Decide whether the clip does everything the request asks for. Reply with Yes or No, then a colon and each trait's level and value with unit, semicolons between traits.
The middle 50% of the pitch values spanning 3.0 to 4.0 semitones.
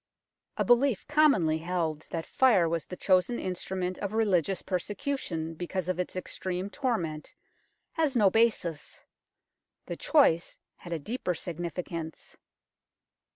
No: average, 4.8 semitones